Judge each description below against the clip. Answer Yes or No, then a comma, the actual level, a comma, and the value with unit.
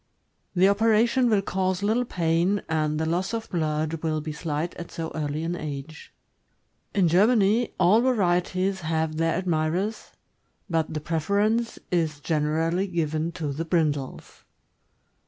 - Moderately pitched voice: Yes, medium, 170 Hz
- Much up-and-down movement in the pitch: No, average, 3.9 semitones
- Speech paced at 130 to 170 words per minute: Yes, average, 140 wpm